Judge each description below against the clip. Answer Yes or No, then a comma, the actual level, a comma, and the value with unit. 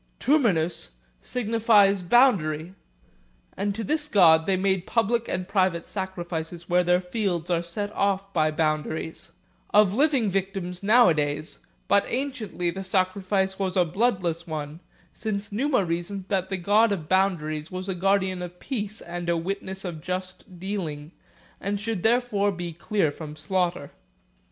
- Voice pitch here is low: No, high, 190 Hz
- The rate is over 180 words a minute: No, average, 145 wpm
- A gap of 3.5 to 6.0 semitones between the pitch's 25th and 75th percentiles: No, average, 3.1 semitones